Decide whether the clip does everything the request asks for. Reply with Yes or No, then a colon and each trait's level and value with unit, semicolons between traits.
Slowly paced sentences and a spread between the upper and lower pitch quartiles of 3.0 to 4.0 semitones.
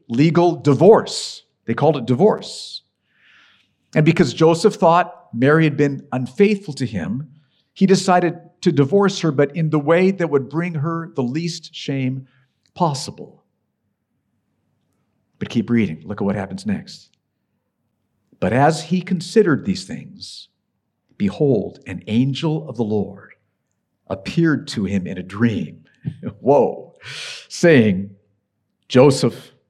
No: slow, 125 wpm; average, 5.2 semitones